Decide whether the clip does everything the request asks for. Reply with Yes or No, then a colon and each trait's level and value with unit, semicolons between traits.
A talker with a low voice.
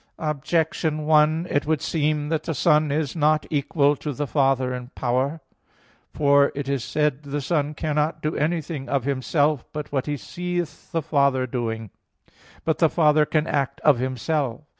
No: medium, 150 Hz